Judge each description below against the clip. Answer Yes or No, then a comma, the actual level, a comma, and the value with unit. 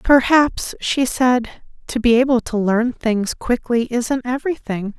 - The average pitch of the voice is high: Yes, high, 245 Hz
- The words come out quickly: No, average, 145 wpm